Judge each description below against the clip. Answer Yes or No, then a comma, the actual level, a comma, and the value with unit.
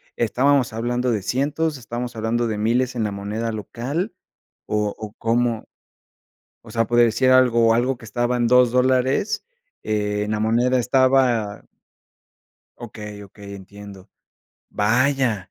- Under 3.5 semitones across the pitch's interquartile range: Yes, average, 2.9 semitones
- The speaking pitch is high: No, low, 120 Hz